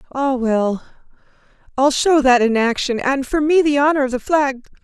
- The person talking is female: Yes, female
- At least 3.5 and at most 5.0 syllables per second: Yes, 4.9 syllables/s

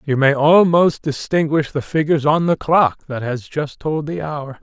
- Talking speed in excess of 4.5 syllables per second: No, 4.4 syllables/s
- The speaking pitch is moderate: Yes, medium, 150 Hz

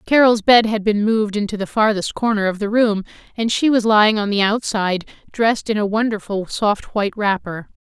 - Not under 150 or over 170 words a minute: No, average, 200 wpm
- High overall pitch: Yes, high, 210 Hz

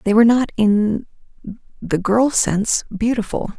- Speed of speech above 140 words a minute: No, slow, 135 wpm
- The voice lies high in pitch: Yes, high, 215 Hz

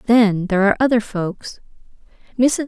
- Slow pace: Yes, slow, 110 wpm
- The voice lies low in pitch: No, high, 220 Hz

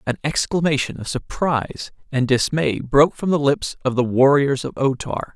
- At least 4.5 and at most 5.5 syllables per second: Yes, 5.0 syllables/s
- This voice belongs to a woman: No, male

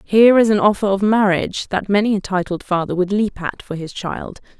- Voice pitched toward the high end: Yes, high, 195 Hz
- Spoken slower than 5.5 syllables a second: No, 5.6 syllables/s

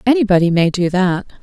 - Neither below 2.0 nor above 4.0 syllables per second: No, 5.8 syllables/s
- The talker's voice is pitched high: Yes, high, 195 Hz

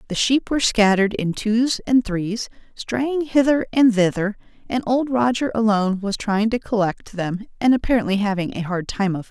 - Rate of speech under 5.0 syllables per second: No, 5.1 syllables/s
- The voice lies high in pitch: Yes, high, 220 Hz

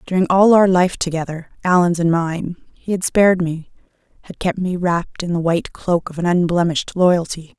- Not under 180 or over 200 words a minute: Yes, average, 190 wpm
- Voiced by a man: No, female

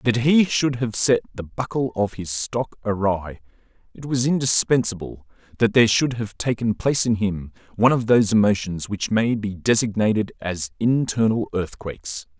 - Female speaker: No, male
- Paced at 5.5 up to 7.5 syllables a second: No, 5.0 syllables/s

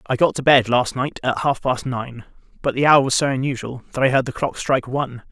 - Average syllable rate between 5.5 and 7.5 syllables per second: Yes, 5.8 syllables/s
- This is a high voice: No, low, 130 Hz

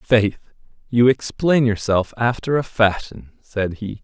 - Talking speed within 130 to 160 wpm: Yes, slow, 135 wpm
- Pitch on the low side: Yes, low, 115 Hz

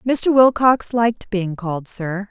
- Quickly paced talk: No, average, 155 wpm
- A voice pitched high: Yes, high, 215 Hz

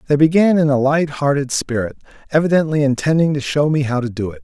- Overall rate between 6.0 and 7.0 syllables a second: Yes, 6.2 syllables/s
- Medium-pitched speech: Yes, medium, 145 Hz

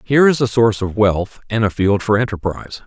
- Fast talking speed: Yes, fast, 230 wpm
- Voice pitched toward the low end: Yes, low, 110 Hz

